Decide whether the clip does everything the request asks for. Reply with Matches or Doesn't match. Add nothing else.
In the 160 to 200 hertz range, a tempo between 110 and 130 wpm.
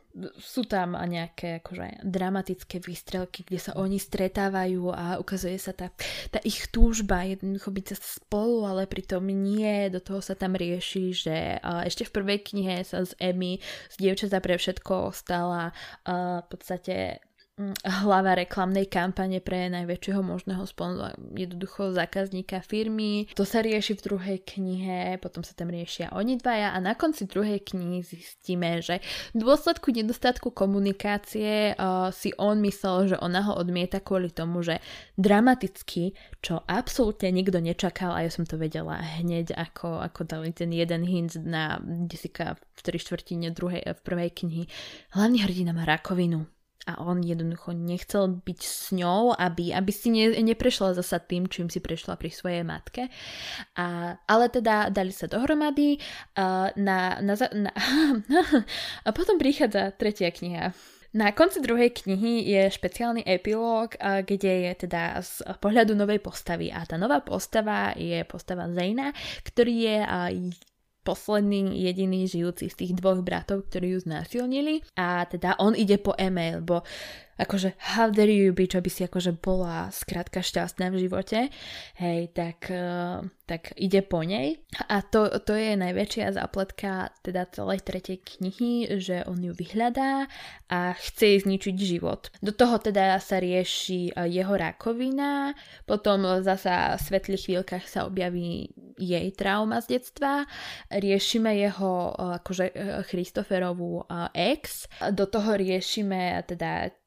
Doesn't match